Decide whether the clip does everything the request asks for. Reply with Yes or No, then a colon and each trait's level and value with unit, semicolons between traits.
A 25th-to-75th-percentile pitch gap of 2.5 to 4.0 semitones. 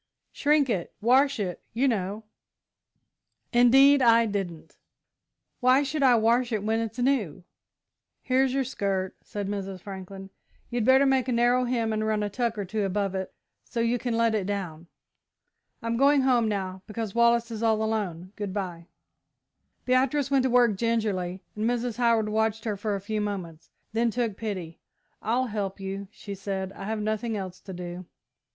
Yes: average, 3.7 semitones